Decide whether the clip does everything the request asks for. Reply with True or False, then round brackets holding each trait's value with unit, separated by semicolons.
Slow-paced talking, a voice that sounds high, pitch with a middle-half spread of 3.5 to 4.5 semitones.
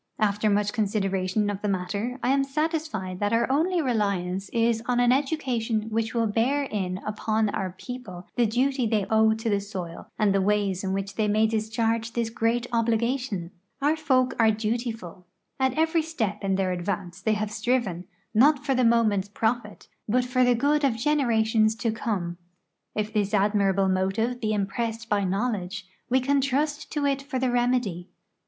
False (175 wpm; 220 Hz; 3.8 semitones)